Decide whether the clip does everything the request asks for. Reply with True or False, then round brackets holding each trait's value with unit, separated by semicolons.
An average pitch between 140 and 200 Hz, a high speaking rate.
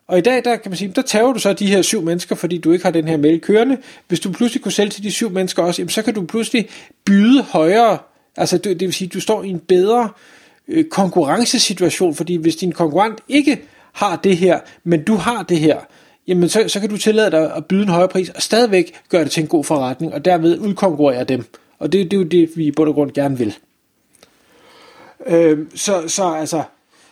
True (185 Hz; 230 wpm)